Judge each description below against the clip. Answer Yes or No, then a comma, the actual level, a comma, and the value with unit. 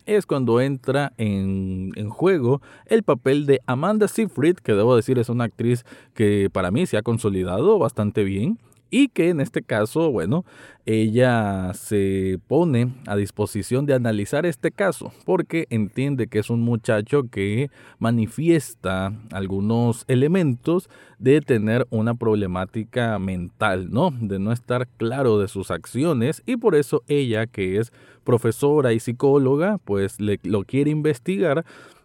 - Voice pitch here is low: Yes, low, 120 Hz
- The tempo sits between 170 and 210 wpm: No, average, 145 wpm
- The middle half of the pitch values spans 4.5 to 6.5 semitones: Yes, wide, 5.4 semitones